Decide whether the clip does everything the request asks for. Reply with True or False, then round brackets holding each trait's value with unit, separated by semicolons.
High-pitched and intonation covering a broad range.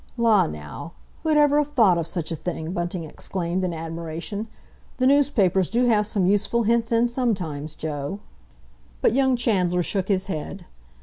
True (195 Hz; 5.8 semitones)